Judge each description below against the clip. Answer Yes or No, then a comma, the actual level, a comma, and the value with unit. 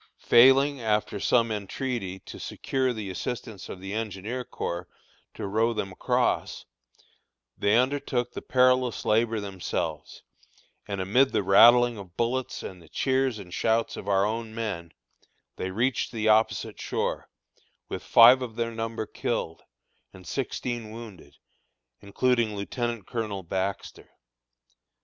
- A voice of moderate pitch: No, low, 110 Hz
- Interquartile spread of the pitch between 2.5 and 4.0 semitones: Yes, average, 3.7 semitones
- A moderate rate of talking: No, slow, 130 wpm